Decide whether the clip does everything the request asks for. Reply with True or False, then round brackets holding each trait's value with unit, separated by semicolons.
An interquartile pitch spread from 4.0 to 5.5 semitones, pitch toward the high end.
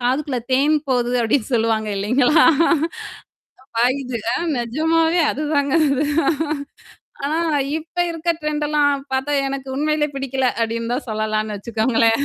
True (4.3 semitones; 265 Hz)